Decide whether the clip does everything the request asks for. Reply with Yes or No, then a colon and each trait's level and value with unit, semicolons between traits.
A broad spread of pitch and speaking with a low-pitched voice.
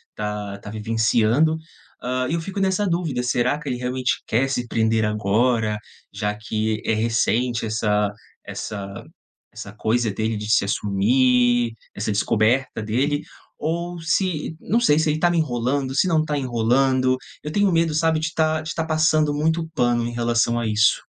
Yes: wide, 5.9 semitones; low, 125 Hz